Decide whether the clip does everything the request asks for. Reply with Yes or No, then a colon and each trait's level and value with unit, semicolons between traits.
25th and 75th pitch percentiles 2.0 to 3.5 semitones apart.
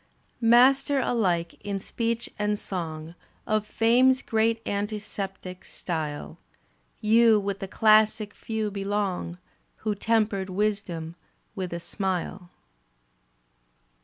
Yes: average, 3.1 semitones